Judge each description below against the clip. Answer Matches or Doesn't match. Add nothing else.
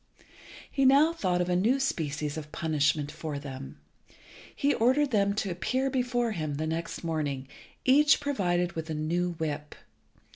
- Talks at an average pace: Matches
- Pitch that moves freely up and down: Matches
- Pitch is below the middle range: Doesn't match